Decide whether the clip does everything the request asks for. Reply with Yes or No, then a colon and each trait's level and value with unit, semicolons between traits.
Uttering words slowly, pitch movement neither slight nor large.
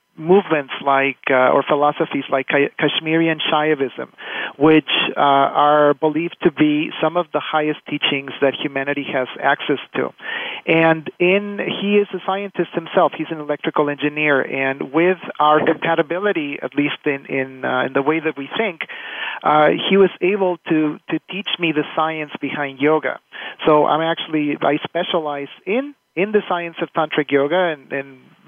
No: average, 160 wpm; average, 3.3 semitones